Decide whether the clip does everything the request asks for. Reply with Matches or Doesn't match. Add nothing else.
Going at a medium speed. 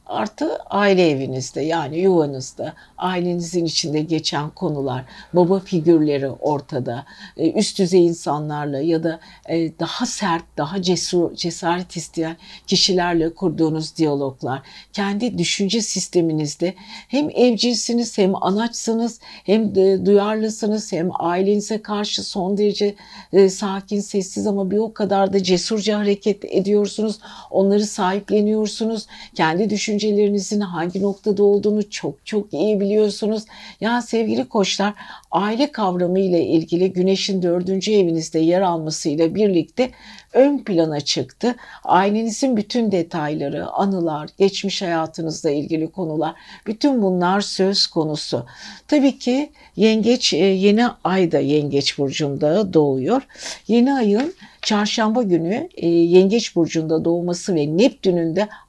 Matches